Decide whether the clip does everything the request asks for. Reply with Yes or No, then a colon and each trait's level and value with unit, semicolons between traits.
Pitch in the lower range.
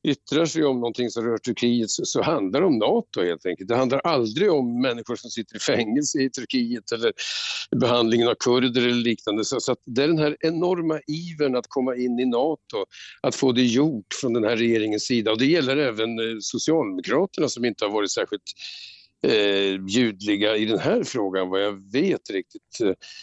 Yes: low, 125 Hz